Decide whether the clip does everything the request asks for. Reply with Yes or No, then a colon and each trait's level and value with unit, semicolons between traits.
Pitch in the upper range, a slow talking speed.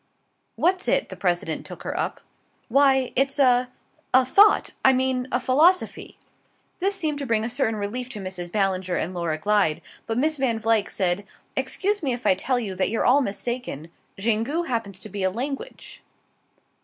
No: high, 240 Hz; average, 180 wpm